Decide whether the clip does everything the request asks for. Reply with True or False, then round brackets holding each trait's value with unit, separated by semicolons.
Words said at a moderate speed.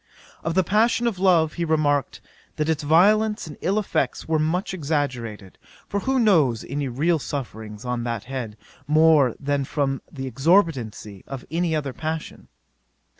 True (160 wpm)